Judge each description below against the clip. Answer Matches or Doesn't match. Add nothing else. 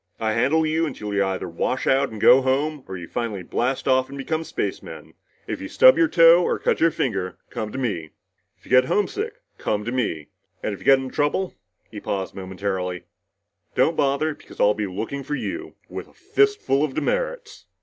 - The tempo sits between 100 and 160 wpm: Doesn't match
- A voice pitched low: Matches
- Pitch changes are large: Matches